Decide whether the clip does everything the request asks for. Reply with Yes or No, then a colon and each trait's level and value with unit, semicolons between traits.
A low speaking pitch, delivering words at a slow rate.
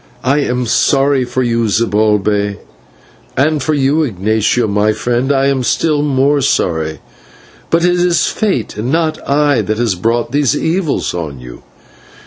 No: low, 125 Hz; average, 150 wpm